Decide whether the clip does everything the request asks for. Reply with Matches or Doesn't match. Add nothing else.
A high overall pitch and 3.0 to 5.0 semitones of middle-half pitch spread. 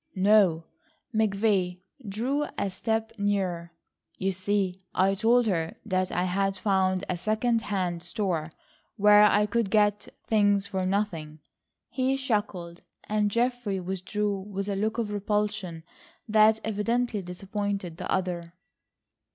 Doesn't match